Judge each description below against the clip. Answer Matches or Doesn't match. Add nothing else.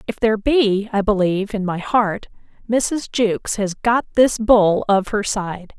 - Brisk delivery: Doesn't match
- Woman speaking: Matches